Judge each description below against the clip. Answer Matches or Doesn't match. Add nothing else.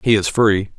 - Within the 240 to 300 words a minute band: Doesn't match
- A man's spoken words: Matches